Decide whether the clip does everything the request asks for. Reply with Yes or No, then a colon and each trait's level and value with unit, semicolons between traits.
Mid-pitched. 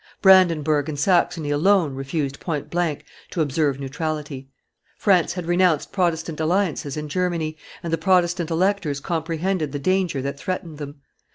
Yes: medium, 160 Hz